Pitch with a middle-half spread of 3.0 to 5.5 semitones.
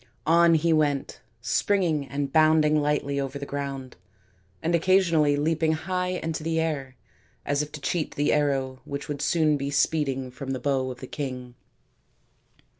No: narrow, 2.6 semitones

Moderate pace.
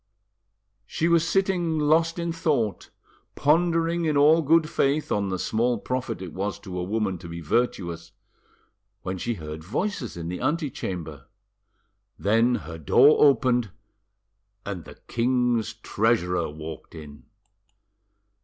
No: slow, 130 wpm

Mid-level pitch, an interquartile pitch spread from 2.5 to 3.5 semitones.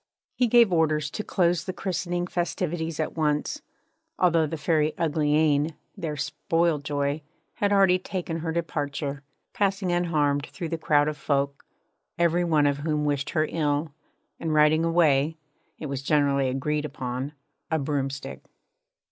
Yes: medium, 155 Hz; average, 2.8 semitones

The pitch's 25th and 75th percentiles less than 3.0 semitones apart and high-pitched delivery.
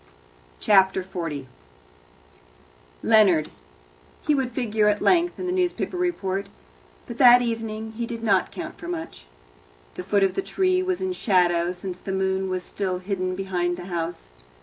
No: wide, 5.6 semitones; high, 200 Hz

